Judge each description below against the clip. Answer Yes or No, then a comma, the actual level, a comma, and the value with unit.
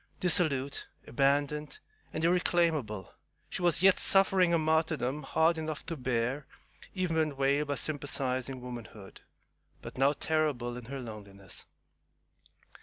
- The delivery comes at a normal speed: No, slow, 120 wpm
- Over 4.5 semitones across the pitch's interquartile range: No, average, 4.1 semitones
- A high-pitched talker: No, medium, 145 Hz